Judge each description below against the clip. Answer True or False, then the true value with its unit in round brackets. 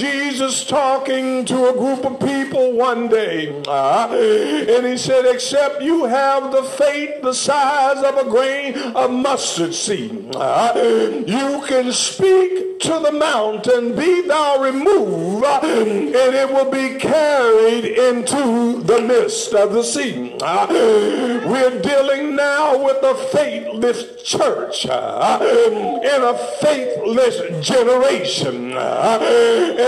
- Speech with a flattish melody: False (3.0 semitones)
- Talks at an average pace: False (125 wpm)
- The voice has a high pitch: True (270 Hz)